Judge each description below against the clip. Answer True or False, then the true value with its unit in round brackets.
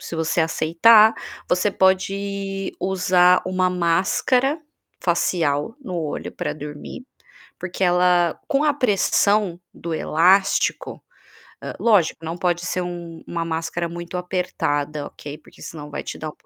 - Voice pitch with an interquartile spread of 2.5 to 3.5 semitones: True (2.8 semitones)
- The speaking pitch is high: False (180 Hz)